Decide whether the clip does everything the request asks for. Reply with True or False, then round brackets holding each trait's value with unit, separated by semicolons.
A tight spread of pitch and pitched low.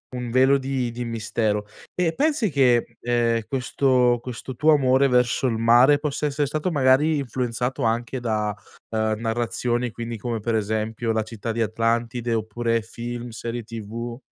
True (2.3 semitones; 120 Hz)